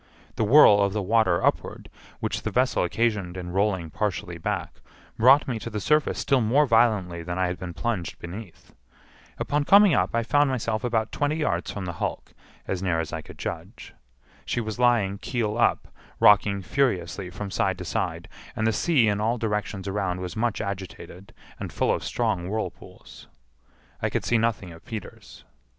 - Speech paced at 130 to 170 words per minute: No, average, 180 wpm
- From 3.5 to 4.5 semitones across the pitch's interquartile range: Yes, average, 4.2 semitones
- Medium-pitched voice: No, low, 105 Hz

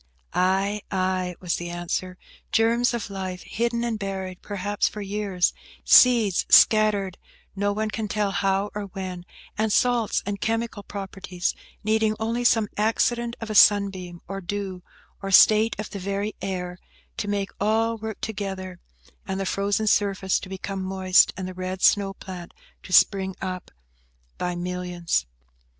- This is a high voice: Yes, high, 195 Hz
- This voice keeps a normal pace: Yes, average, 150 wpm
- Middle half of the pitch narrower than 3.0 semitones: Yes, narrow, 2.4 semitones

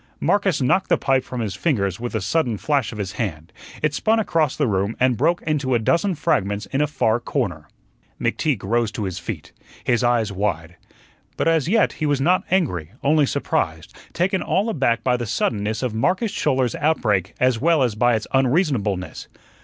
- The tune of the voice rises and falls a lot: Yes, wide, 6.6 semitones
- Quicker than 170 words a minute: Yes, average, 190 wpm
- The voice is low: Yes, low, 125 Hz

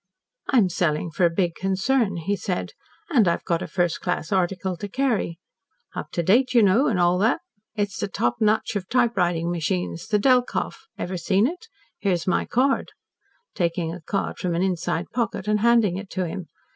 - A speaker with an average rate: Yes, average, 185 wpm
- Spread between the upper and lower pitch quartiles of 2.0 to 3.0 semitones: No, average, 4.1 semitones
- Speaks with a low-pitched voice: No, high, 190 Hz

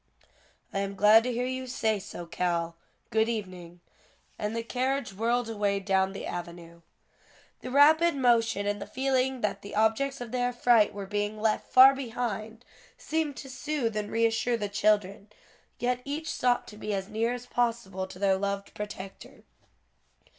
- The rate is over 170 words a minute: No, average, 165 wpm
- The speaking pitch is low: No, high, 220 Hz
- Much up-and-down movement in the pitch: No, average, 3.7 semitones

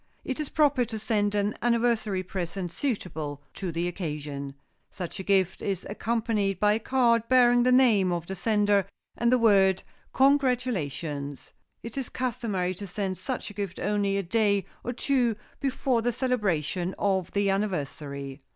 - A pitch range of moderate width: Yes, average, 4.6 semitones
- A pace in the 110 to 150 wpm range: No, average, 160 wpm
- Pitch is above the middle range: Yes, high, 205 Hz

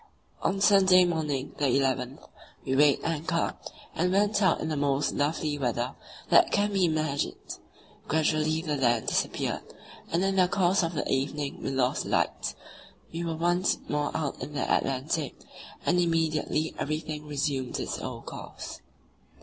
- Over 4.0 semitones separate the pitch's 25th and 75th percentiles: No, average, 3.5 semitones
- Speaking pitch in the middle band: Yes, medium, 155 Hz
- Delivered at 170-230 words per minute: No, average, 155 wpm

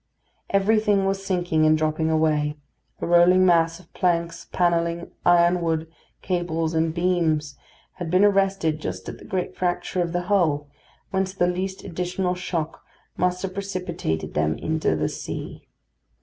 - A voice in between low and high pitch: Yes, medium, 175 Hz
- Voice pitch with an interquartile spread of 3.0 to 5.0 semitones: No, narrow, 2.5 semitones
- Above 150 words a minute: No, average, 145 wpm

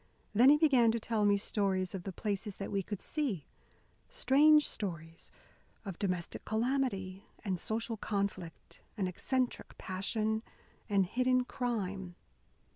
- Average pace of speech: No, slow, 130 wpm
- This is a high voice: Yes, high, 205 Hz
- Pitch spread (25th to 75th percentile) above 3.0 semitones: Yes, average, 4.4 semitones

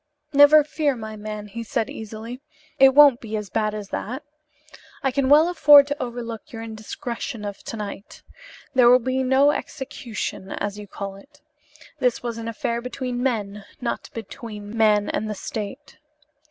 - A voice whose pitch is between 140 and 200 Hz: No, high, 235 Hz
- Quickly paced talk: No, average, 165 wpm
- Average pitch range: Yes, average, 3.9 semitones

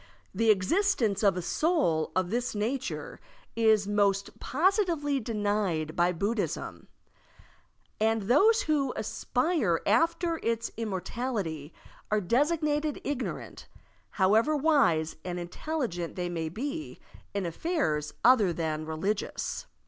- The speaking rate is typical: No, slow, 110 wpm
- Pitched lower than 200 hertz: No, high, 220 Hz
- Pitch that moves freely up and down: Yes, wide, 8.1 semitones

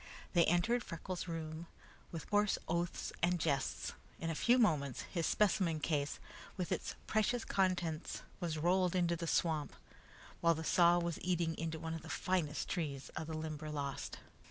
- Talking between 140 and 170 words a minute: Yes, average, 160 wpm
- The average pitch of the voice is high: No, medium, 170 Hz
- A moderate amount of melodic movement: No, narrow, 2.2 semitones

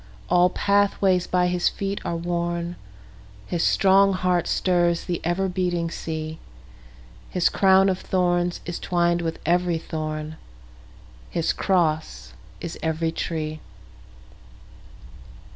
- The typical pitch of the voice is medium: Yes, medium, 170 Hz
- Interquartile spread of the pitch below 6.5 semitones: Yes, narrow, 2.5 semitones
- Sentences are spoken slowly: Yes, slow, 100 wpm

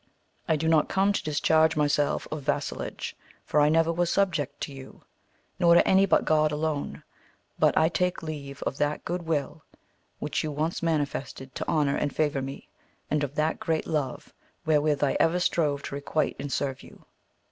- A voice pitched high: No, medium, 150 Hz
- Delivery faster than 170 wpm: Yes, average, 180 wpm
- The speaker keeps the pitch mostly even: Yes, narrow, 2.1 semitones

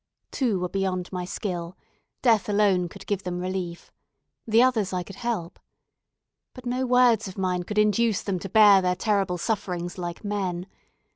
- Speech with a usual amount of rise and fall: Yes, average, 3.1 semitones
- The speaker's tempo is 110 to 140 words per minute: No, average, 165 wpm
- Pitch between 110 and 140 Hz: No, high, 195 Hz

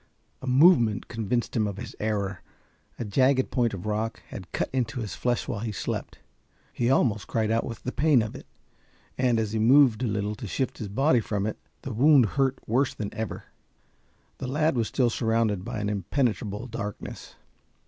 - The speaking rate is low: No, average, 190 wpm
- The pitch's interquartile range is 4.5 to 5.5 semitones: No, average, 3.4 semitones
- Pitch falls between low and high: No, low, 115 Hz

